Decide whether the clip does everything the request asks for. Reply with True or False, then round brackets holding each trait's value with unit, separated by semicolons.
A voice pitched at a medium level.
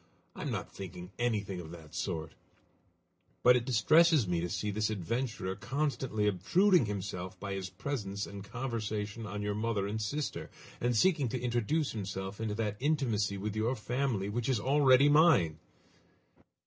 False (110 Hz)